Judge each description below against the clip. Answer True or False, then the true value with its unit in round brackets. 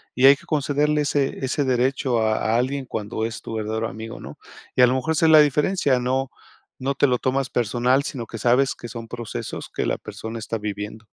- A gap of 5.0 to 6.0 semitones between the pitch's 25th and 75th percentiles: False (3.5 semitones)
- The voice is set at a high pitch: False (125 Hz)